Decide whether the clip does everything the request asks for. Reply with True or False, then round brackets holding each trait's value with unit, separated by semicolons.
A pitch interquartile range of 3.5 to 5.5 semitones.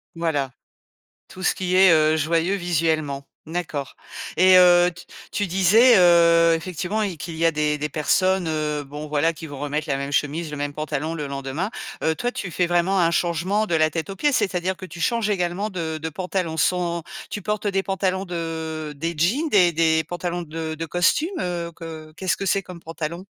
False (2.9 semitones)